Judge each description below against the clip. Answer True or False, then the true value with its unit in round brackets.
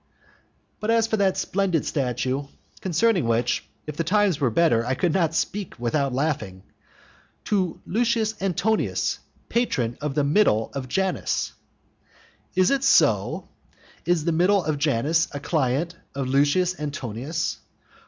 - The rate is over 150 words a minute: False (135 wpm)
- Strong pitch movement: True (6.0 semitones)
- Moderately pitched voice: True (160 Hz)